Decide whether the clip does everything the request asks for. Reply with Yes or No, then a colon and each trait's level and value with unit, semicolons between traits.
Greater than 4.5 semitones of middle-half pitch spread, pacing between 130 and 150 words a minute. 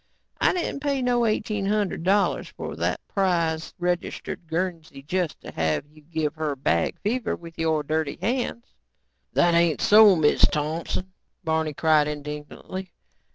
No: average, 4.2 semitones; average, 145 wpm